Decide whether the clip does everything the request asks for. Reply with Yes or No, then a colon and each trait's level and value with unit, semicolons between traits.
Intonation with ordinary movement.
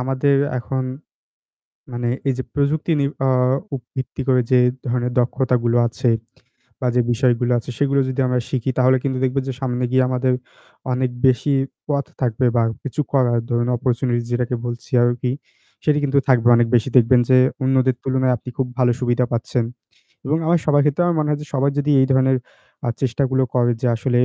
No: narrow, 1.8 semitones